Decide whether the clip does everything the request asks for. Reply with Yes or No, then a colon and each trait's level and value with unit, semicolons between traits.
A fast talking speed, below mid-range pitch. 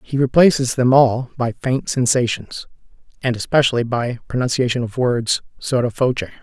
No: average, 140 wpm; low, 125 Hz